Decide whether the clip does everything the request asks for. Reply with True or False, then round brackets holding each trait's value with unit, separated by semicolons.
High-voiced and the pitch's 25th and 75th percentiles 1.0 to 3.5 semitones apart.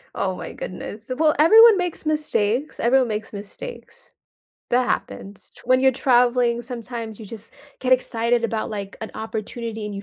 True (235 Hz; 3.0 semitones)